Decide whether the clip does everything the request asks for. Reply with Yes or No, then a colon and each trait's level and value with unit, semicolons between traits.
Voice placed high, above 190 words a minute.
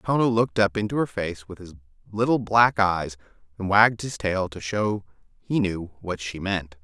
No: low, 100 Hz; average, 200 wpm